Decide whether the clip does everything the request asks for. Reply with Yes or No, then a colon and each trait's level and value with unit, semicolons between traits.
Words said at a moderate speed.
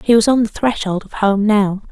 No: fast, 250 wpm